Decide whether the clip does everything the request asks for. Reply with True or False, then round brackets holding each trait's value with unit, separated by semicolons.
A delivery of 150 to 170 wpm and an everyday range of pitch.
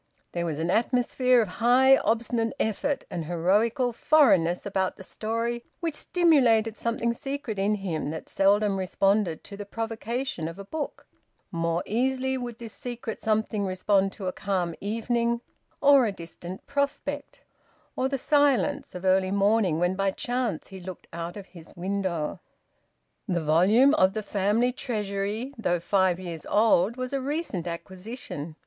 True (155 wpm; 4.7 semitones)